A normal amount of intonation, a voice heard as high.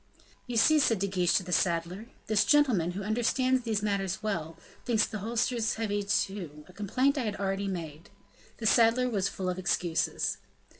Yes: average, 3.9 semitones; high, 205 Hz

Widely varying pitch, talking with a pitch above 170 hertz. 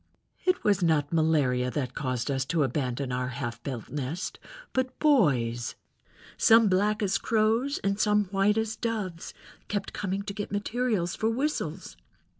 Yes: wide, 8.0 semitones; high, 190 Hz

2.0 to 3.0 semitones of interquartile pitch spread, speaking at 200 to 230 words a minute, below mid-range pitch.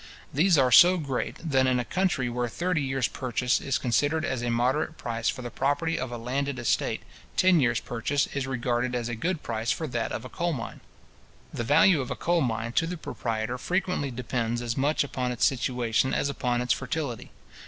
No: average, 3.6 semitones; fast, 205 wpm; low, 130 Hz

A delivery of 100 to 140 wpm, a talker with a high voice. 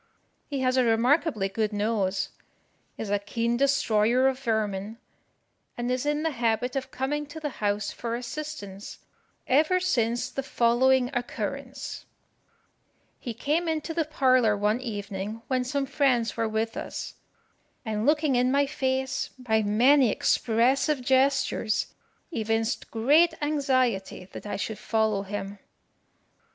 Yes: slow, 135 wpm; high, 245 Hz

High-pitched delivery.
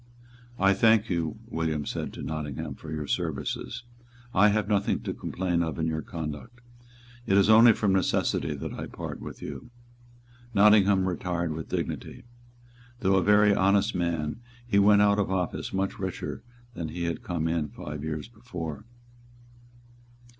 No: very low, 95 Hz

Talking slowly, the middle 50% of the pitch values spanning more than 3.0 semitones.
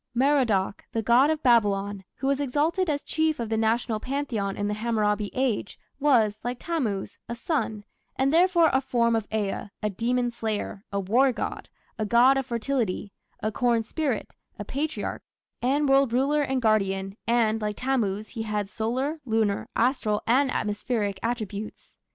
No: average, 165 wpm; average, 4.2 semitones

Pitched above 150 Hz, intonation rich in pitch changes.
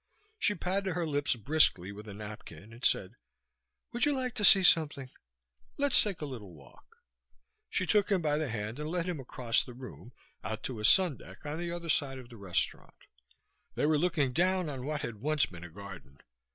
No: medium, 145 Hz; wide, 7.9 semitones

